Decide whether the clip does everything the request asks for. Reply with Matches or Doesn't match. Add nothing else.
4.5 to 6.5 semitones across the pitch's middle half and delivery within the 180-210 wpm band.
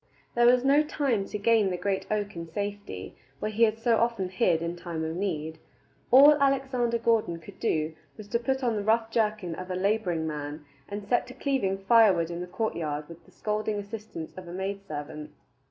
Matches